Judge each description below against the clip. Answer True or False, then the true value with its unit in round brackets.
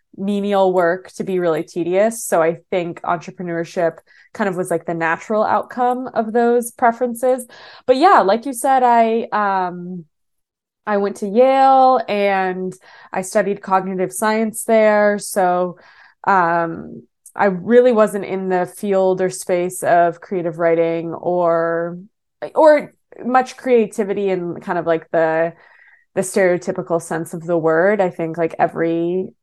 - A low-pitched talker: False (190 Hz)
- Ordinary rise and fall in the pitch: True (4.7 semitones)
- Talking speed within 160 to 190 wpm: False (140 wpm)